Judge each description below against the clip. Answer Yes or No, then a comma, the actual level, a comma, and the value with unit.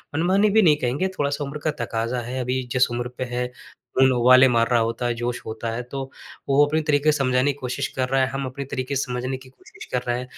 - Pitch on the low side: Yes, low, 130 Hz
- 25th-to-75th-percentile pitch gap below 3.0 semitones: Yes, narrow, 2.4 semitones